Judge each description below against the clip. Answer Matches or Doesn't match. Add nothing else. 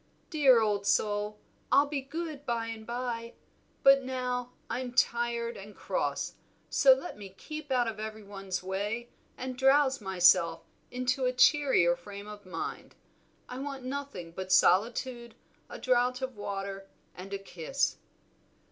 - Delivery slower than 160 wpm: Matches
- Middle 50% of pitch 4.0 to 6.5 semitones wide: Matches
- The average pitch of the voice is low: Doesn't match